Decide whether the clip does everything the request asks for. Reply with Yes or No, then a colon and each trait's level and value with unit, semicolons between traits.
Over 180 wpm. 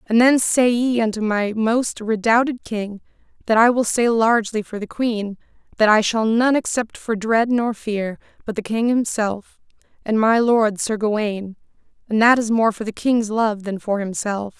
Yes: average, 190 wpm